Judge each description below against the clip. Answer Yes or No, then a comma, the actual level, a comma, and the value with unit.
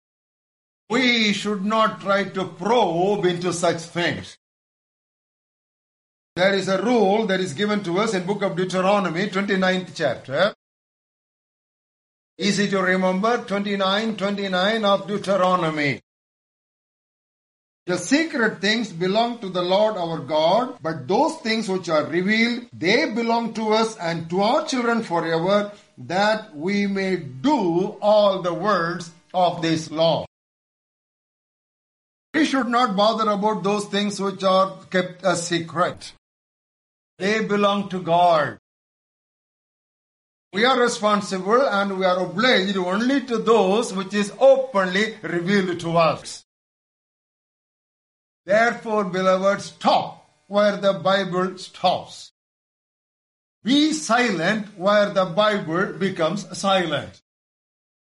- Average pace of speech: No, slow, 115 wpm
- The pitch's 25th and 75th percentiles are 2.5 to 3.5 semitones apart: Yes, average, 3.0 semitones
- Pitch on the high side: Yes, high, 200 Hz